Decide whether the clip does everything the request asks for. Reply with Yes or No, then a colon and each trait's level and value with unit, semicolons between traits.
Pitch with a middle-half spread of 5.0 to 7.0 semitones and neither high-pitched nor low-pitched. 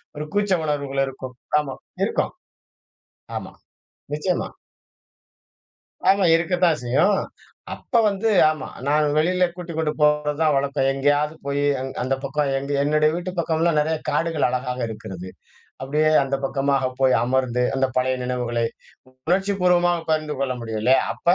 No: average, 3.8 semitones; medium, 150 Hz